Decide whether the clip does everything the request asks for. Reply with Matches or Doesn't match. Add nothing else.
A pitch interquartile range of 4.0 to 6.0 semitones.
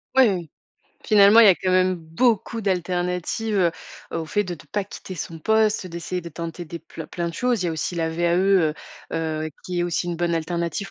Doesn't match